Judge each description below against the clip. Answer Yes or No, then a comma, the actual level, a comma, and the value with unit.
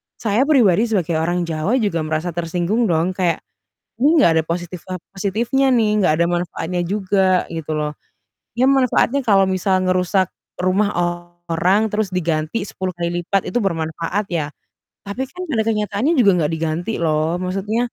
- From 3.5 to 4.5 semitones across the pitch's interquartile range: Yes, average, 4.2 semitones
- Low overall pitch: No, medium, 185 Hz